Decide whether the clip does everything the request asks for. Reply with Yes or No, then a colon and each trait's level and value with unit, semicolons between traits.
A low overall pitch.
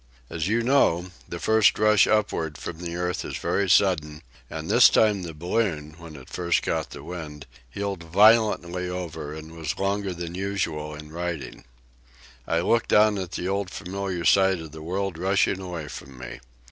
Yes: very low, 90 Hz